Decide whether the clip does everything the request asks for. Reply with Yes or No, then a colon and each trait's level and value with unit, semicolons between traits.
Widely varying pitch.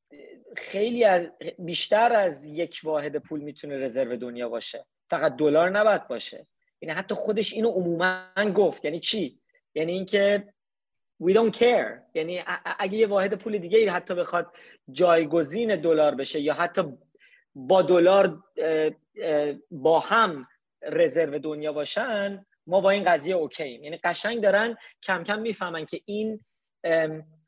No: average, 4.8 semitones